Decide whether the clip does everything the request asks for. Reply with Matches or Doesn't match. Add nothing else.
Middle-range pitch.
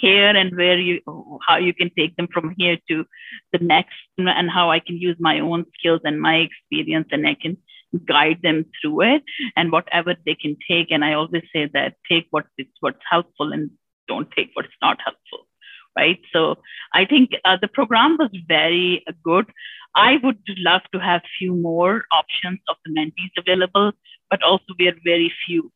Matches